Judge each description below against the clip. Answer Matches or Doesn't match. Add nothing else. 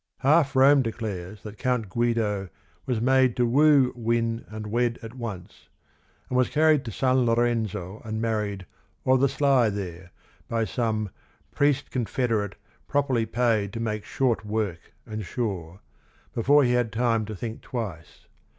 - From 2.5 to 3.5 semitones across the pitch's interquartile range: Matches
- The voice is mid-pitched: Doesn't match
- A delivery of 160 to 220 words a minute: Doesn't match